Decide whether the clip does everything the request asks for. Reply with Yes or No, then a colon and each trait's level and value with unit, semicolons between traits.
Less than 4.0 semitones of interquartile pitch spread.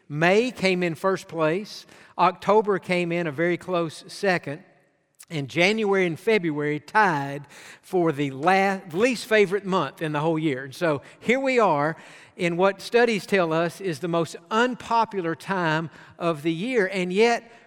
Yes: average, 3.6 semitones